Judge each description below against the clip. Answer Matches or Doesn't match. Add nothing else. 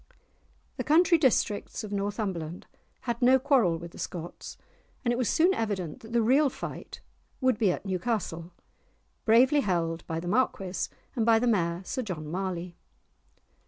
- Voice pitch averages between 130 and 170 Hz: Doesn't match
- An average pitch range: Doesn't match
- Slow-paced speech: Doesn't match